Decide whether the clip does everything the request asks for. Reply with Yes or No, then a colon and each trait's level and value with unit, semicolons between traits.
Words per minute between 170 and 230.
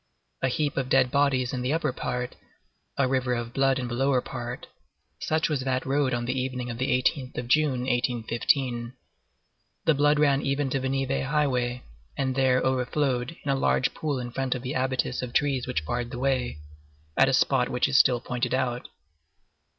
Yes: average, 190 wpm